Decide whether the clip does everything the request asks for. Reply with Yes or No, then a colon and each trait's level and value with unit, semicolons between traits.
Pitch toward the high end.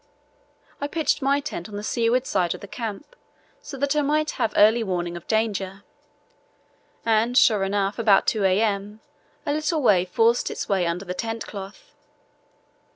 Yes: high, 215 Hz